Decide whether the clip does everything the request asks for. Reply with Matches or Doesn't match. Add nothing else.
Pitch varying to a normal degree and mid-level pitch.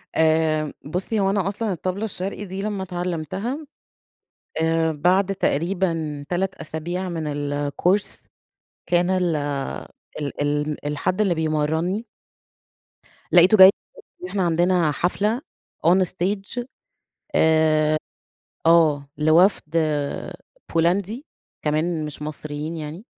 Matches